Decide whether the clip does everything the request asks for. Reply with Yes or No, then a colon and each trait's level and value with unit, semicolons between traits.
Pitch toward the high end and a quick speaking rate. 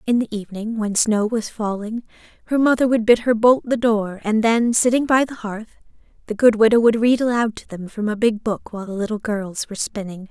Yes: high, 220 Hz; fast, 225 wpm